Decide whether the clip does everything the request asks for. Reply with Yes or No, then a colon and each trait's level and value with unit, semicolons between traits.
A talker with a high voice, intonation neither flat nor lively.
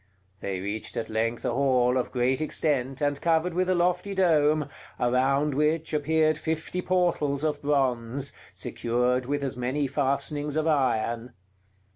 No: medium, 140 Hz; average, 3.8 semitones